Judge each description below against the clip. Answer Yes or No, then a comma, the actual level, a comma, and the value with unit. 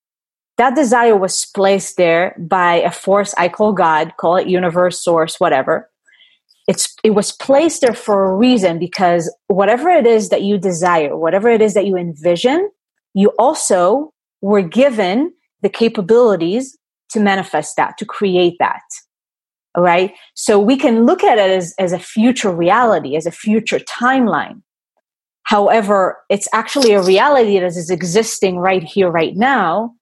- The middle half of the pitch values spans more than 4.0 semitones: Yes, average, 4.8 semitones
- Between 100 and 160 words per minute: Yes, average, 155 wpm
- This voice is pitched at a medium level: No, high, 200 Hz